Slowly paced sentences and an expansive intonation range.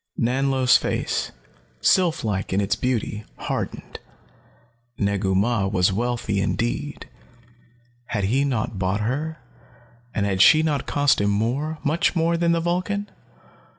Yes: slow, 130 wpm; wide, 7.3 semitones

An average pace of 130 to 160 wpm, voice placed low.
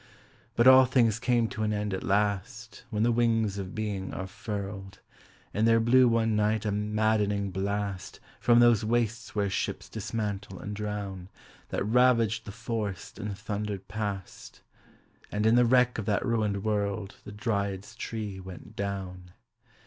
Yes: average, 155 wpm; low, 105 Hz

